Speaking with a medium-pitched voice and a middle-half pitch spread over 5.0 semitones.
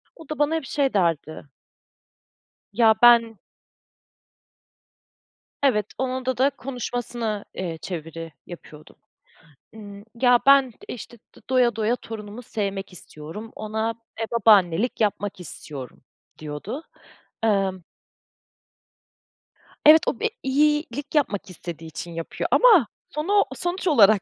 No: high, 225 Hz; wide, 5.6 semitones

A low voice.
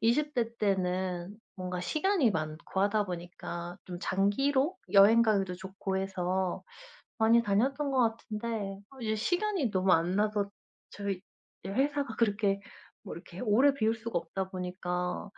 No: high, 200 Hz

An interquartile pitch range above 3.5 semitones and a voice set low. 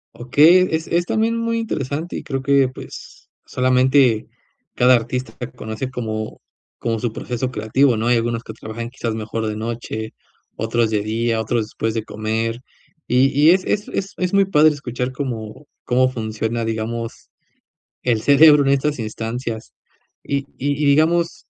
Yes: average, 4.0 semitones; low, 125 Hz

